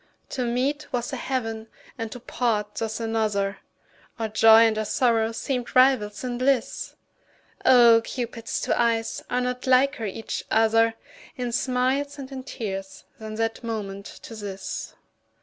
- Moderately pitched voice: No, high, 230 Hz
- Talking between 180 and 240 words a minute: No, average, 150 wpm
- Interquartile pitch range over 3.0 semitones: No, narrow, 2.4 semitones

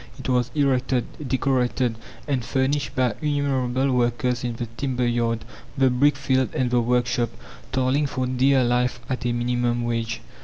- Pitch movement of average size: No, narrow, 1.6 semitones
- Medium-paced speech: Yes, average, 155 wpm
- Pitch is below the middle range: Yes, low, 125 Hz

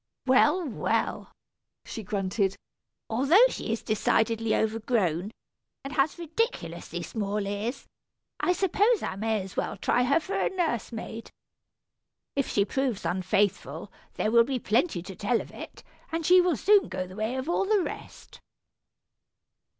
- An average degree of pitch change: No, wide, 7.6 semitones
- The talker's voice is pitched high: Yes, high, 235 Hz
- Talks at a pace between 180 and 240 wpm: No, average, 150 wpm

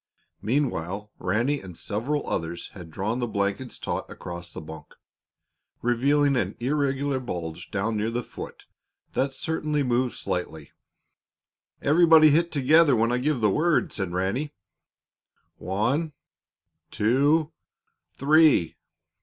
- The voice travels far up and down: Yes, wide, 6.8 semitones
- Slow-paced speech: Yes, slow, 120 wpm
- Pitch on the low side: Yes, low, 120 Hz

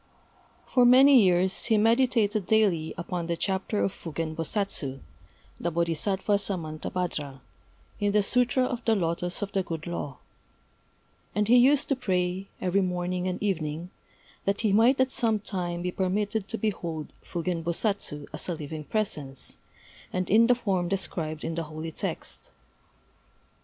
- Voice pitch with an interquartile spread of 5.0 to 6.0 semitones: No, average, 4.3 semitones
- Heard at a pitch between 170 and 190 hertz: Yes, medium, 185 Hz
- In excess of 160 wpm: No, average, 150 wpm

